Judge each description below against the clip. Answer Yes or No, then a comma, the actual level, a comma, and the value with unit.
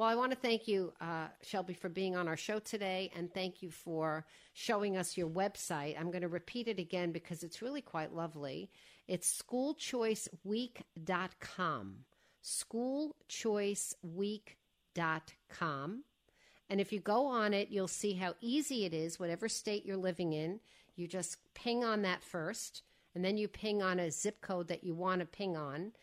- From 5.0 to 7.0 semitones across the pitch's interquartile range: No, average, 3.7 semitones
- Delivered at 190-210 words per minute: No, average, 170 wpm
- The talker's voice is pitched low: No, medium, 185 Hz